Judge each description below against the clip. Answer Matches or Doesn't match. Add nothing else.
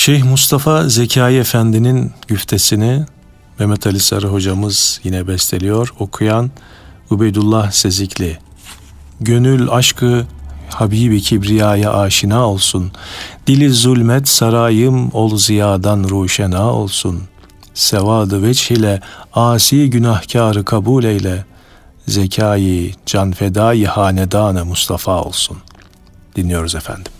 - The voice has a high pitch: Doesn't match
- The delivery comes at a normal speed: Doesn't match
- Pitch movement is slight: Doesn't match